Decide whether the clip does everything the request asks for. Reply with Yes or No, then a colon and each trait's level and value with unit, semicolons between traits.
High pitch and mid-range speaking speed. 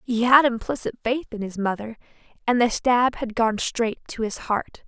Yes: high, 235 Hz; average, 195 wpm